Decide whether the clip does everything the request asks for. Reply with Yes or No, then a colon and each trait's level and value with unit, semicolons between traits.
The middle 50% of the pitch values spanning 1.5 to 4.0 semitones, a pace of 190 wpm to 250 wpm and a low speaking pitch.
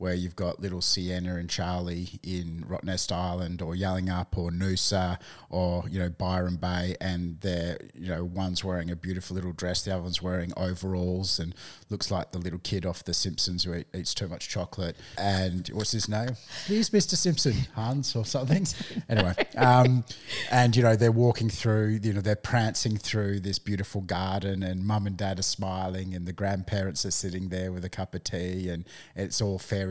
Yes: average, 2.7 semitones; average, 195 wpm; very low, 95 Hz